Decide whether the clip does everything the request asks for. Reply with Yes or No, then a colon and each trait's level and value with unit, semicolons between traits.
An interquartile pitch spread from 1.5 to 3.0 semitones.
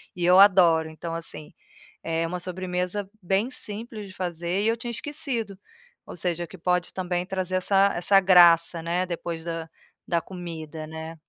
Yes: narrow, 2.5 semitones